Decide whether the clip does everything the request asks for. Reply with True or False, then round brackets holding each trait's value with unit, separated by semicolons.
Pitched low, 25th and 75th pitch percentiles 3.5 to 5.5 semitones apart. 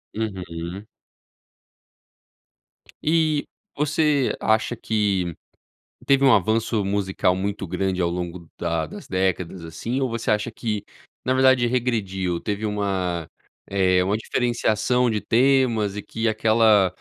True (105 Hz; 4.2 semitones)